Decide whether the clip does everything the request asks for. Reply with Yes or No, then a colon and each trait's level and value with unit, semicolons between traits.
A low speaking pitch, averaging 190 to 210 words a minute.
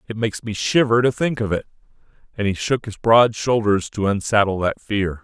Yes: low, 110 Hz; fast, 205 wpm